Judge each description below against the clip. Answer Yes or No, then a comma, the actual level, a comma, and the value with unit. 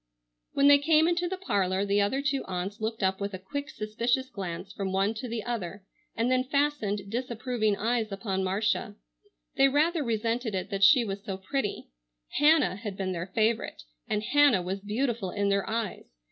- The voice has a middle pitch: No, high, 215 Hz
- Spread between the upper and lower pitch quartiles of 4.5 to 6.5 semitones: Yes, average, 4.8 semitones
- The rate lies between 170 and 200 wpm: Yes, average, 185 wpm